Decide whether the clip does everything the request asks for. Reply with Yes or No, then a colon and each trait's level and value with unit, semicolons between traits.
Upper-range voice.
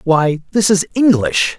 No: medium, 180 Hz